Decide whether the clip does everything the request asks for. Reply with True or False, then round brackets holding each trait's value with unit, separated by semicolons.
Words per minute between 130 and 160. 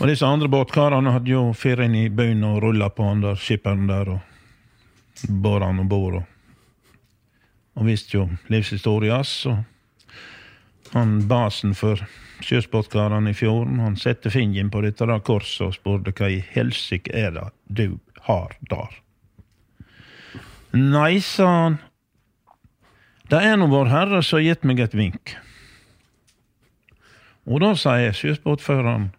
True (140 wpm)